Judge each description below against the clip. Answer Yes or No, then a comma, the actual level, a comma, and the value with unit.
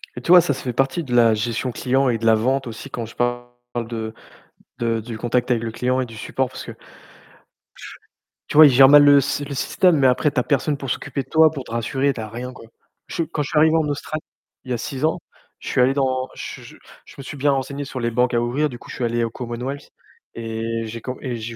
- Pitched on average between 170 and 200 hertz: No, low, 125 Hz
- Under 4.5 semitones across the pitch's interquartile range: Yes, average, 3.1 semitones